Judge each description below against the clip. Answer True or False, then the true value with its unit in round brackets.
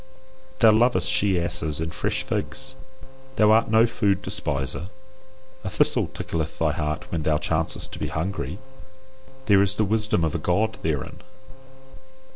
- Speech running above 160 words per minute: False (150 wpm)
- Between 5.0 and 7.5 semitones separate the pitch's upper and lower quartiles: True (5.4 semitones)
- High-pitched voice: False (95 Hz)